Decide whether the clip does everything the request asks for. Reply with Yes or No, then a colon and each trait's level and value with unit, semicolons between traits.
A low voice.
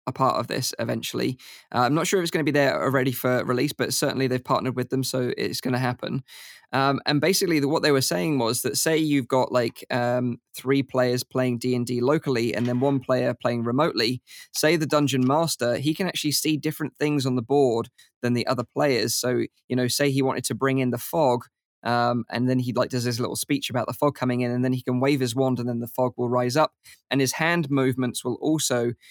Yes: low, 130 Hz